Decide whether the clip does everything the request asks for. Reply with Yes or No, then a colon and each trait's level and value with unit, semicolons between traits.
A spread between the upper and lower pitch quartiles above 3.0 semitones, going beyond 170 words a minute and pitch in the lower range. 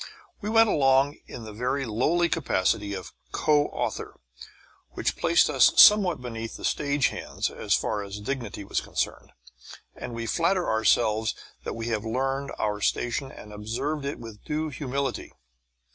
No: average, 4.8 semitones; average, 155 wpm; low, 125 Hz